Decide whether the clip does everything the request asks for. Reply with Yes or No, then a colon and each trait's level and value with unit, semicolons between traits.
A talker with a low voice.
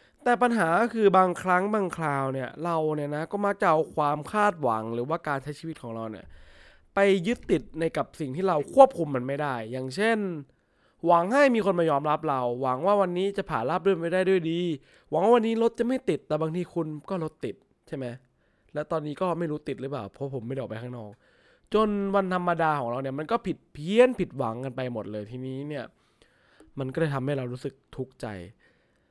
No: medium, 155 Hz